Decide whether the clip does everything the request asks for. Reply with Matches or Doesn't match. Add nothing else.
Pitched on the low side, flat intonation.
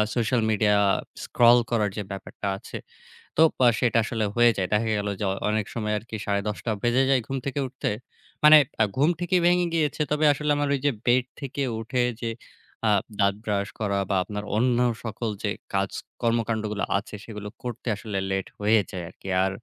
Doesn't match